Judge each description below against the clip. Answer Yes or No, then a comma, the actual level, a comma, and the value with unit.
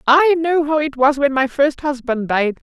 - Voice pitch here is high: Yes, very high, 280 Hz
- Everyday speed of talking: No, fast, 220 wpm